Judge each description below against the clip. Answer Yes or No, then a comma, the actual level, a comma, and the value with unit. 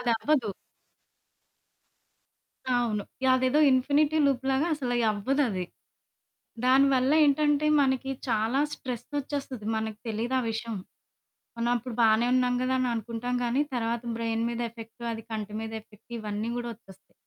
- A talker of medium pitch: No, high, 240 Hz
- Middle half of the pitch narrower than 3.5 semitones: Yes, average, 2.9 semitones